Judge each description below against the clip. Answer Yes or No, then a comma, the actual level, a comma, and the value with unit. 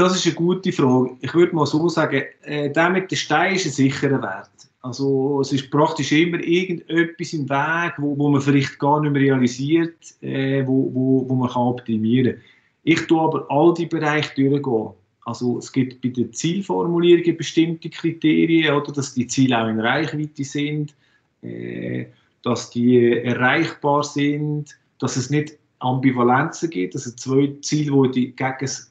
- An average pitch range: Yes, average, 3.7 semitones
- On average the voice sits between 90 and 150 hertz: Yes, medium, 140 Hz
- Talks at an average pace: Yes, average, 170 wpm